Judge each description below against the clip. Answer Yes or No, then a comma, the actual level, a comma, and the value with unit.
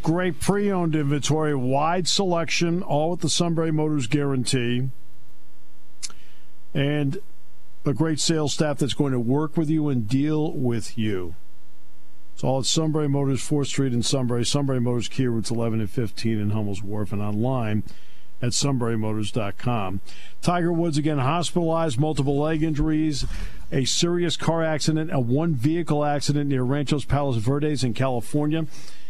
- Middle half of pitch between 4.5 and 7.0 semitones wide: Yes, wide, 5.5 semitones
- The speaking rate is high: No, average, 140 wpm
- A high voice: No, medium, 140 Hz